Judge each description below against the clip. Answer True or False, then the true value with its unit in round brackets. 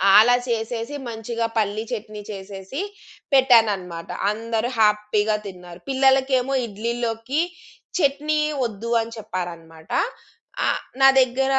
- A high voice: True (225 Hz)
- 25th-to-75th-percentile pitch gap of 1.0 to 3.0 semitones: False (3.5 semitones)